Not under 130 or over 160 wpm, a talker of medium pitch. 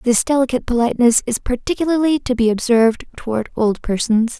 No: average, 150 wpm; high, 245 Hz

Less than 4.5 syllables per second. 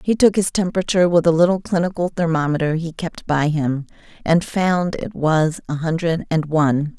No: 5.2 syllables/s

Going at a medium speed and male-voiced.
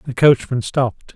Yes: average, 155 wpm; male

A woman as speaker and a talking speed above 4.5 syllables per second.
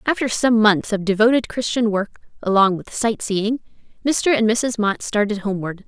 Yes: female; 5.1 syllables/s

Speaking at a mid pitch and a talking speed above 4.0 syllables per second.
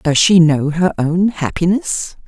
No: medium, 170 Hz; 3.8 syllables/s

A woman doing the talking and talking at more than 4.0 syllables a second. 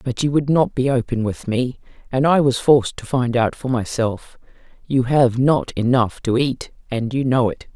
Yes: female; 4.6 syllables/s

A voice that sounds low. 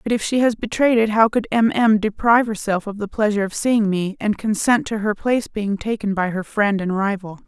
No: high, 210 Hz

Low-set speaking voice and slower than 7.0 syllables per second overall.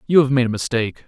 No: low, 130 Hz; 7.7 syllables/s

